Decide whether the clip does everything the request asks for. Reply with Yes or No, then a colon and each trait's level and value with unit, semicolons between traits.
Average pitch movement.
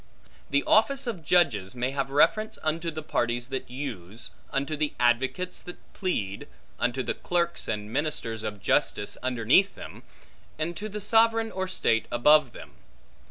No: wide, 6.9 semitones